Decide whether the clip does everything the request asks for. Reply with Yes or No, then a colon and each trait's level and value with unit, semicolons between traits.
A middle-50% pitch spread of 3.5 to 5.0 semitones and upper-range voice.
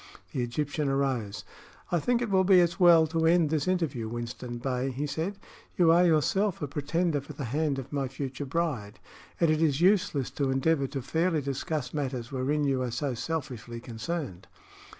No: average, 4.3 semitones; medium, 145 Hz